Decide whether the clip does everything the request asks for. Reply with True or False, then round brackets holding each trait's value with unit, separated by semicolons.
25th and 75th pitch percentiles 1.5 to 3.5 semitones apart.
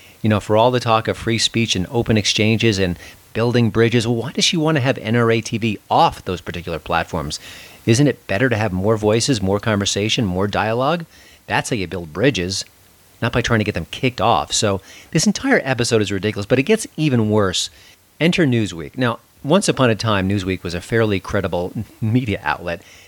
False (4.2 semitones)